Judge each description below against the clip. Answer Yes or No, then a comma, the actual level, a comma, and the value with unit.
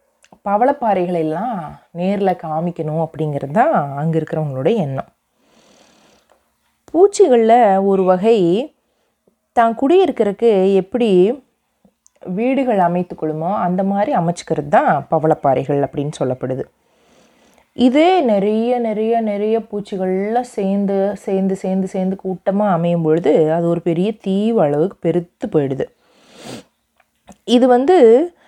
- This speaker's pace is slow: No, average, 95 wpm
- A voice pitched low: No, high, 195 Hz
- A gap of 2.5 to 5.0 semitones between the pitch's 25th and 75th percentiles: No, wide, 5.4 semitones